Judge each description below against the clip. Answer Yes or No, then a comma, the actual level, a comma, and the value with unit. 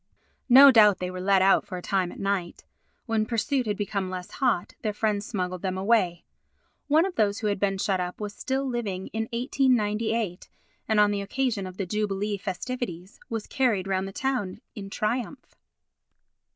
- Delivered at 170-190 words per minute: Yes, average, 180 wpm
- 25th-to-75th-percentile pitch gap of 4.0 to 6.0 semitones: No, average, 3.6 semitones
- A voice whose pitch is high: Yes, high, 205 Hz